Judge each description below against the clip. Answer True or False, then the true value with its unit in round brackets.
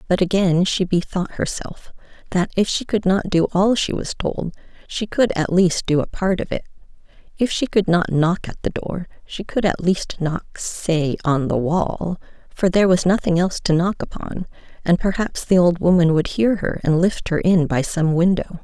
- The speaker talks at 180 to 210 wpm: True (195 wpm)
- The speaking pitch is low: False (180 Hz)